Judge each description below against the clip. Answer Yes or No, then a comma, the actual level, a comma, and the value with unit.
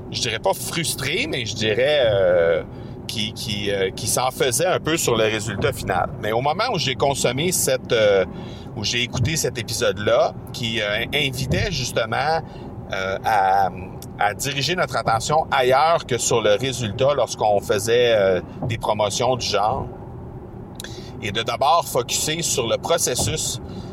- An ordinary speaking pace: Yes, average, 155 wpm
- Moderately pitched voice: No, low, 130 Hz